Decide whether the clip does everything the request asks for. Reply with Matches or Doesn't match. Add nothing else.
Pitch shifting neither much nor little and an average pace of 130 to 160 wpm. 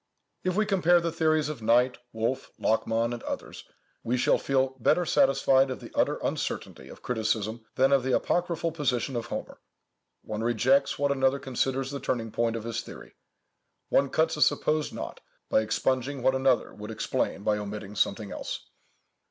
Doesn't match